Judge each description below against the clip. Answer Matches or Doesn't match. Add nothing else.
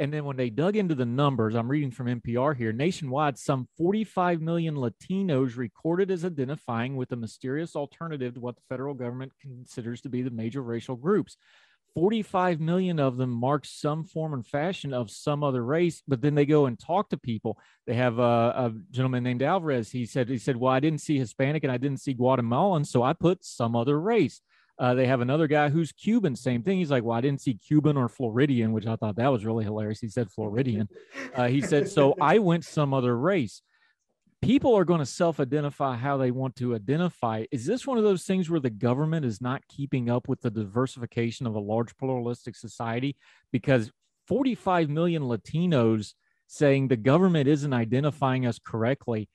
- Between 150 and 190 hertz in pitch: Doesn't match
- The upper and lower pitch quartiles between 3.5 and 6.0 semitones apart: Matches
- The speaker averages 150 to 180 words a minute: Doesn't match